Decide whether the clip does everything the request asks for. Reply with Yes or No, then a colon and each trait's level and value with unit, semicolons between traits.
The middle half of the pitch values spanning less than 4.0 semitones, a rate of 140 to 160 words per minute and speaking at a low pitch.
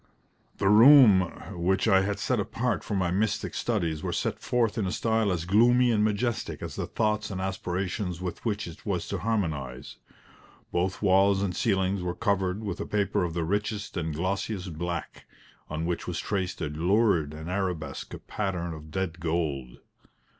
No: average, 3.4 semitones; average, 175 wpm; very low, 95 Hz